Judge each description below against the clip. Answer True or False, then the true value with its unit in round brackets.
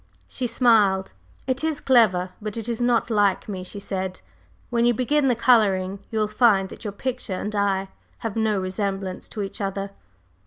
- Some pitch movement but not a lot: True (3.5 semitones)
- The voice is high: True (210 Hz)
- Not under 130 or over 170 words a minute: False (185 wpm)